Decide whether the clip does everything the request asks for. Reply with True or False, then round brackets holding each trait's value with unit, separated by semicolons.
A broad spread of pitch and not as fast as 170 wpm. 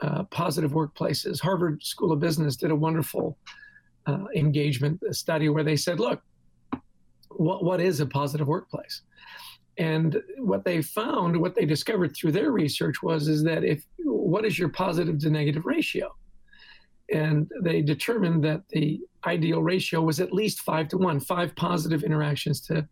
False (2.9 semitones; 160 wpm)